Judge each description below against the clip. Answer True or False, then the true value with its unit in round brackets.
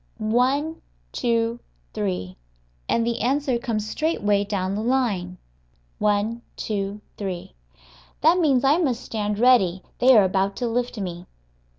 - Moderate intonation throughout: True (4.1 semitones)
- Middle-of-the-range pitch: False (220 Hz)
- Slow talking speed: True (130 wpm)